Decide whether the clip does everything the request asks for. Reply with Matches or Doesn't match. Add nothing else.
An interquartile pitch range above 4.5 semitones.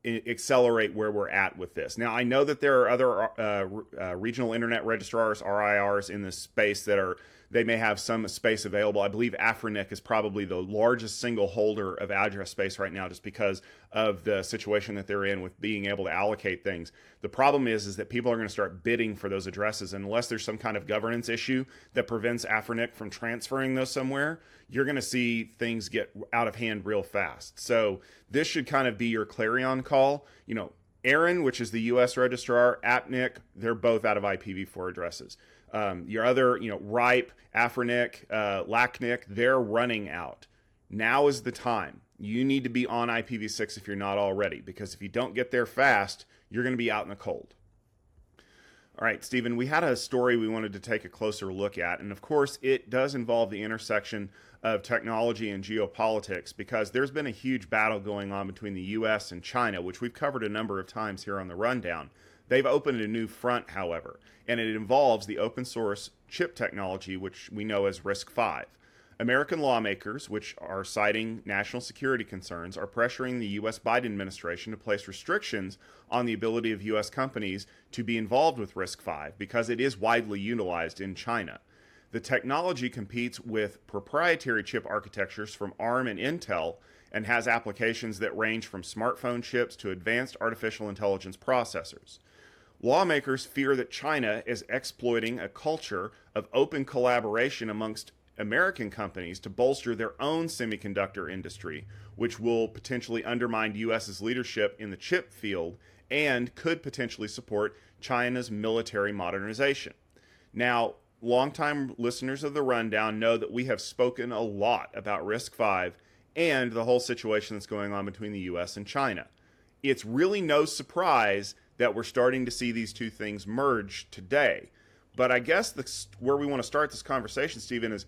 Doesn't match